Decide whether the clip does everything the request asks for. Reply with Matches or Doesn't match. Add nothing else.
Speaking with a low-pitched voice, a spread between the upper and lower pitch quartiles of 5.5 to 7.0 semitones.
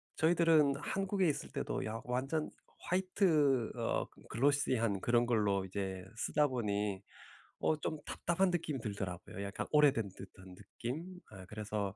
Doesn't match